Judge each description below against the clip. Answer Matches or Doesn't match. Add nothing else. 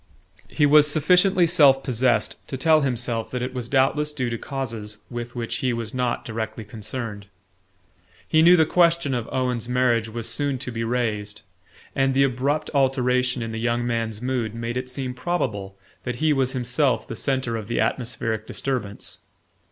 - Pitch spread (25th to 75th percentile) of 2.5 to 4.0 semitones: Matches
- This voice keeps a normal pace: Matches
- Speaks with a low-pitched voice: Matches